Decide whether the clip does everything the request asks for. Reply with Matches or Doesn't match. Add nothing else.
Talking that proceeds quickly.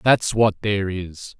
Doesn't match